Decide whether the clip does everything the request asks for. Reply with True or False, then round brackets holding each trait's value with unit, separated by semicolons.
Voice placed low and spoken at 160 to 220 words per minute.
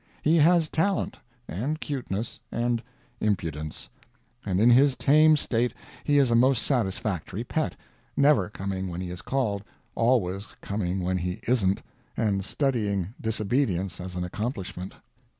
False (110 Hz; 135 wpm)